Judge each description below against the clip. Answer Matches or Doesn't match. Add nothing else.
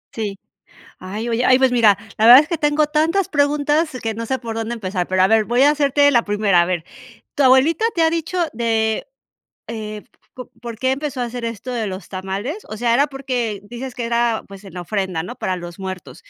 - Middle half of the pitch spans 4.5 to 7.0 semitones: Matches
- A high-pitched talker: Matches